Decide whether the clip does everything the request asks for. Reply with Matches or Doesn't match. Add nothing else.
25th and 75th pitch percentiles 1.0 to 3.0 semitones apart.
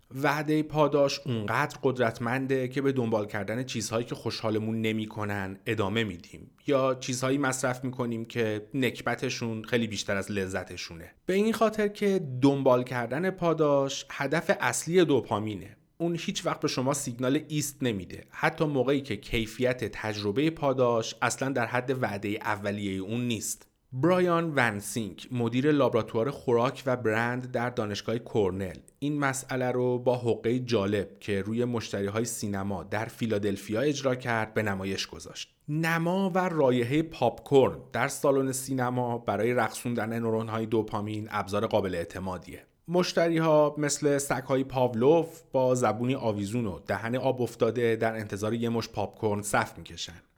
Doesn't match